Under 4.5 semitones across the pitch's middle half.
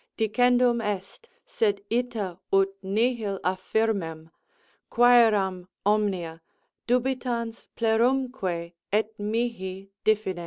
Yes: average, 3.9 semitones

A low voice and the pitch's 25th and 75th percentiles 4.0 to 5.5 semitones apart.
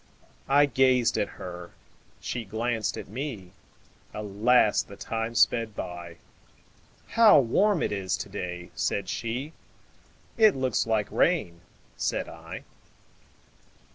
Yes: low, 115 Hz; average, 5.0 semitones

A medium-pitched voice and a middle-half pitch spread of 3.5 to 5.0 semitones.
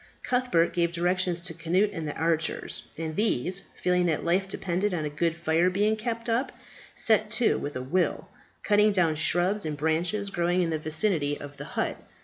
Yes: medium, 175 Hz; average, 4.0 semitones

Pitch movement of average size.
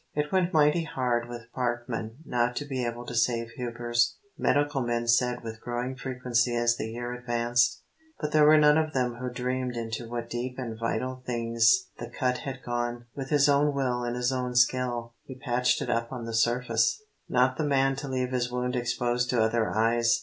No: narrow, 1.5 semitones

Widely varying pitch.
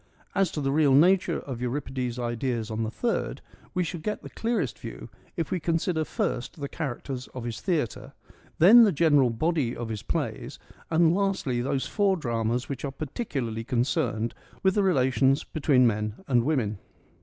Yes: wide, 5.7 semitones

